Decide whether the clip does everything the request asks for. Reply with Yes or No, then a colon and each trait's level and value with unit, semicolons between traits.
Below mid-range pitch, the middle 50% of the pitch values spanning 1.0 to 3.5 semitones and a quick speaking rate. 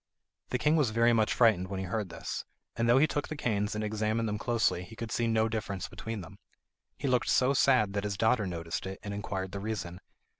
Yes: low, 110 Hz; average, 3.0 semitones; fast, 230 wpm